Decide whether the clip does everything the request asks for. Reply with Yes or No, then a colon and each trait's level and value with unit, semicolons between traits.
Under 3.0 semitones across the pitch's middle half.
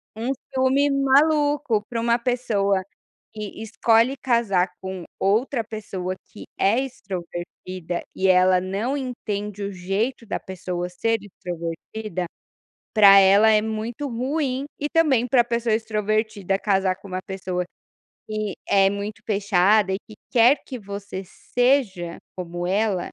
No: average, 3.9 semitones